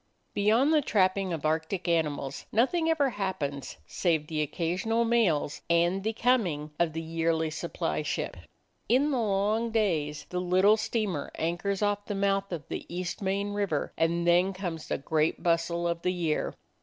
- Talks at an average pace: Yes, average, 160 wpm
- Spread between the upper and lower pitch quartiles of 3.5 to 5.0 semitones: Yes, average, 4.1 semitones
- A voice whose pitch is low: No, medium, 180 Hz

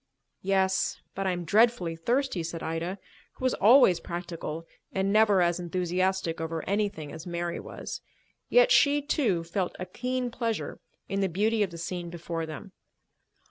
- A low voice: No, medium, 185 Hz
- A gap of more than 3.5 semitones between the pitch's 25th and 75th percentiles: Yes, average, 4.1 semitones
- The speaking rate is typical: Yes, average, 160 wpm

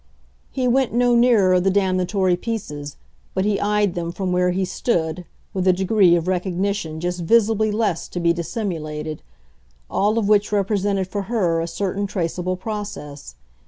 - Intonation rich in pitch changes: No, average, 3.2 semitones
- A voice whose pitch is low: No, high, 190 Hz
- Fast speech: No, average, 160 wpm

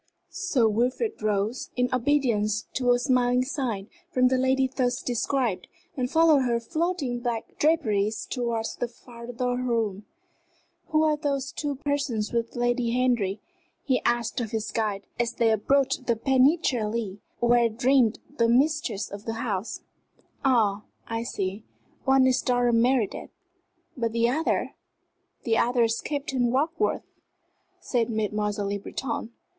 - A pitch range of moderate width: Yes, average, 3.0 semitones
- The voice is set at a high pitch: Yes, high, 245 Hz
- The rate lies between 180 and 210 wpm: No, average, 140 wpm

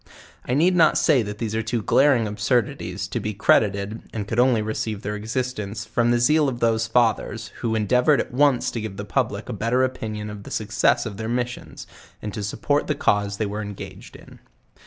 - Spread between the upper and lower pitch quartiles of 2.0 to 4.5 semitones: Yes, average, 3.0 semitones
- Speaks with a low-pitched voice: Yes, low, 115 Hz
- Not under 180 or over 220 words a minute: Yes, fast, 205 wpm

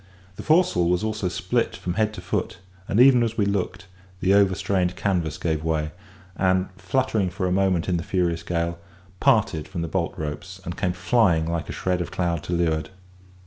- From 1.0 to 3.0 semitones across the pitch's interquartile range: Yes, narrow, 2.6 semitones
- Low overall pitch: Yes, very low, 90 Hz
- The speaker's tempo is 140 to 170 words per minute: No, average, 190 wpm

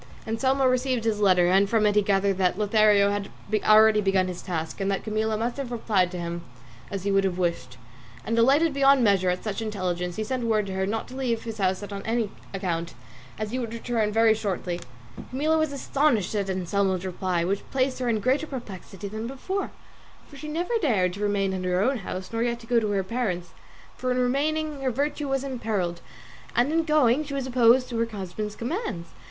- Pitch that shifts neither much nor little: Yes, average, 4.9 semitones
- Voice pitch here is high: Yes, high, 215 Hz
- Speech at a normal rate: No, fast, 210 wpm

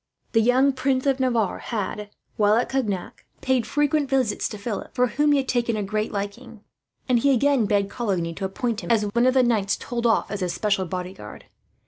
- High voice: Yes, high, 230 Hz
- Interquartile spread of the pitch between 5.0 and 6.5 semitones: No, average, 4.2 semitones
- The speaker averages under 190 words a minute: No, fast, 205 wpm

